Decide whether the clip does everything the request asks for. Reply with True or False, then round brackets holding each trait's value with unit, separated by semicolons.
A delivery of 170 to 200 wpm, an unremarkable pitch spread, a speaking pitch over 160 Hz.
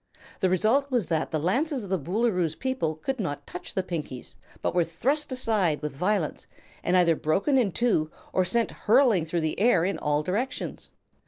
False (185 wpm; 6.7 semitones; 185 Hz)